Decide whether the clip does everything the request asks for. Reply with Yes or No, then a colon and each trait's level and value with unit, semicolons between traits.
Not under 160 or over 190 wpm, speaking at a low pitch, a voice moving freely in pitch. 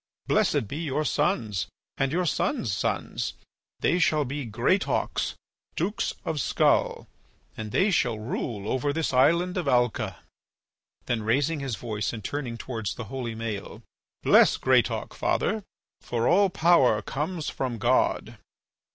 No: slow, 135 wpm; low, 130 Hz; wide, 6.1 semitones